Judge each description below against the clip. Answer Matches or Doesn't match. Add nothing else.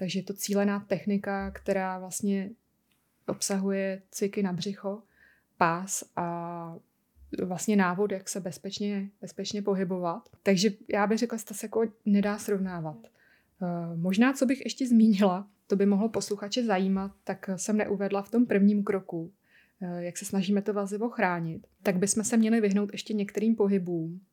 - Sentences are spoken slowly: Doesn't match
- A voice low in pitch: Doesn't match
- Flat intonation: Matches